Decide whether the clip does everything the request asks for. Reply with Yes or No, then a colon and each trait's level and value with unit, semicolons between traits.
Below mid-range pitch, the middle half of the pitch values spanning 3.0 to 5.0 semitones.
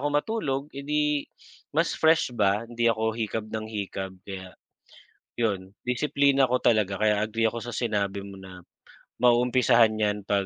Yes: low, 115 Hz; average, 3.8 semitones